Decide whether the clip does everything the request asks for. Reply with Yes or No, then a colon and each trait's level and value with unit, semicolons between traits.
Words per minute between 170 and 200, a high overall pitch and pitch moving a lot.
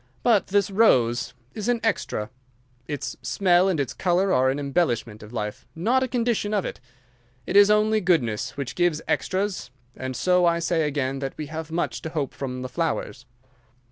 No: average, 180 wpm; medium, 165 Hz; wide, 7.1 semitones